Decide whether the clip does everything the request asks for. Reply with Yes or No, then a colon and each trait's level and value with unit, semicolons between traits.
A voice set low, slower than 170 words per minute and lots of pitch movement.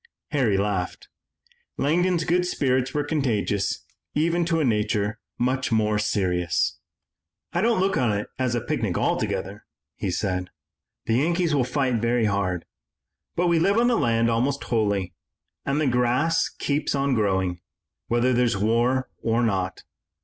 Yes: low, 120 Hz; average, 150 wpm; wide, 5.8 semitones